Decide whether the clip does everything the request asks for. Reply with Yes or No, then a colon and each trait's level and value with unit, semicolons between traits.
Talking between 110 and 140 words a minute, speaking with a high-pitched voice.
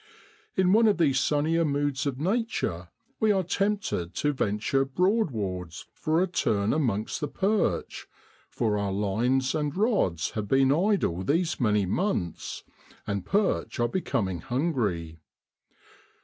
No: slow, 135 wpm; low, 135 Hz